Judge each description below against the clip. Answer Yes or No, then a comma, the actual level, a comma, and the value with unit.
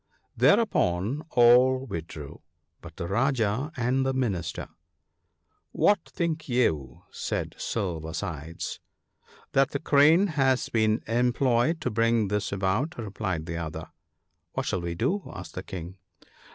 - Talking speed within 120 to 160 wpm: Yes, average, 145 wpm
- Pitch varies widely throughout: Yes, wide, 7.0 semitones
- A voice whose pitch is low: Yes, low, 115 Hz